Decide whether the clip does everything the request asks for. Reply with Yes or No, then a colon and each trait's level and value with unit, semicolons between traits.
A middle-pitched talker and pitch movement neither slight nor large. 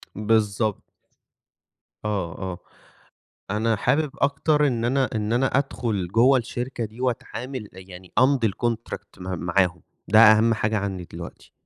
No: low, 110 Hz; average, 4.2 semitones